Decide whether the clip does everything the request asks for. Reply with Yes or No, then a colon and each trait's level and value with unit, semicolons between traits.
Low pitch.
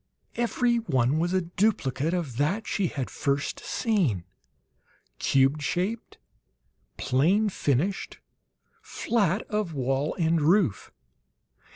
No: medium, 170 Hz